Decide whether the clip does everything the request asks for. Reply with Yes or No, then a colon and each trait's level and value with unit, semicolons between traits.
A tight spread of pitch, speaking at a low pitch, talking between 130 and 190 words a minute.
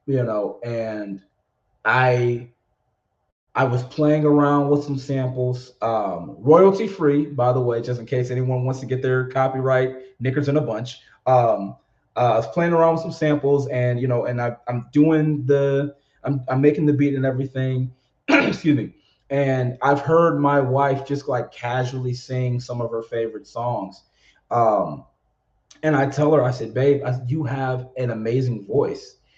Yes: narrow, 2.3 semitones; low, 130 Hz; average, 170 wpm